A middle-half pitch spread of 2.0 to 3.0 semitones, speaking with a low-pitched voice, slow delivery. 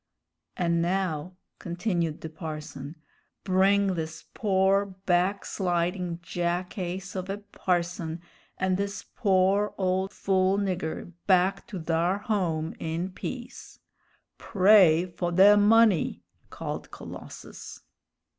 No: narrow, 2.4 semitones; medium, 185 Hz; slow, 105 wpm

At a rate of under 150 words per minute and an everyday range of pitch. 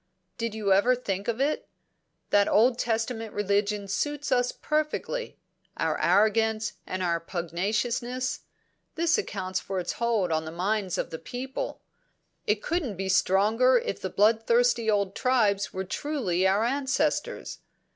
Yes: average, 140 wpm; average, 4.5 semitones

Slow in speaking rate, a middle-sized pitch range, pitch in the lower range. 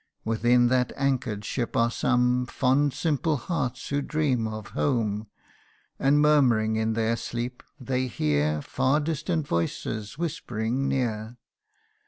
Yes: slow, 125 wpm; average, 3.8 semitones; low, 125 Hz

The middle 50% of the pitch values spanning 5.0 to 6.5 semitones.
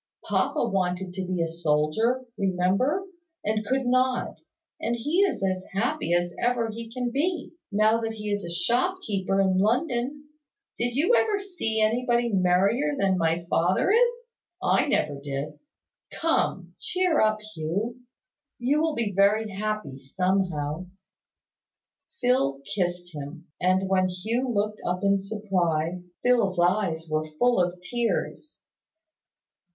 Yes: average, 5.3 semitones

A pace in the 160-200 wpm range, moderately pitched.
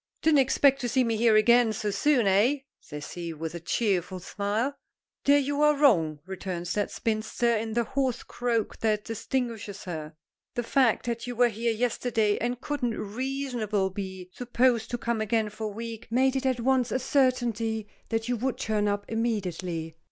No: average, 180 wpm; high, 225 Hz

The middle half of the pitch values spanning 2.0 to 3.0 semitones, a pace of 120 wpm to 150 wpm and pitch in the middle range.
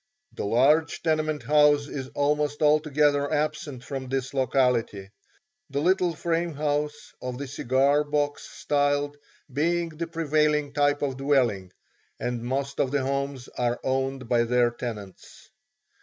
Yes: narrow, 2.5 semitones; slow, 135 wpm; medium, 145 Hz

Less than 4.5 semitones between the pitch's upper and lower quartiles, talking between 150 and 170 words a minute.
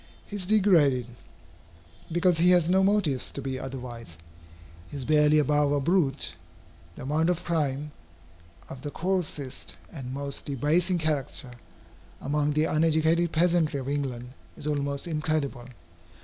No: average, 3.5 semitones; slow, 135 wpm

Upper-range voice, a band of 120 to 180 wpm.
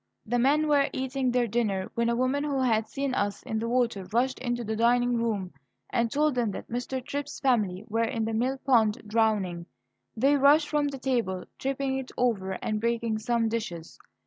No: high, 240 Hz; average, 195 wpm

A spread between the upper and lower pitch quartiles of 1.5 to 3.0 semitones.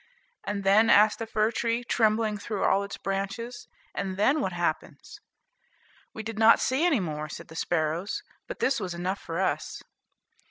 No: average, 3.4 semitones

